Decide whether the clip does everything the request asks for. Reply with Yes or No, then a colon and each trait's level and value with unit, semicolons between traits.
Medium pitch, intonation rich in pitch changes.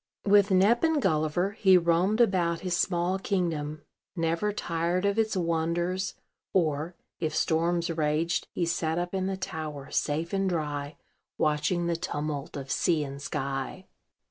No: medium, 170 Hz; average, 3.4 semitones